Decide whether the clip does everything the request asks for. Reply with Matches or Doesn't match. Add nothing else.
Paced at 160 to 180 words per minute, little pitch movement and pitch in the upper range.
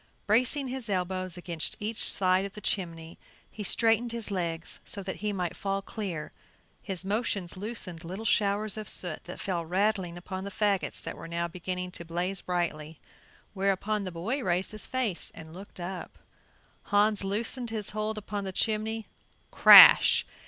Doesn't match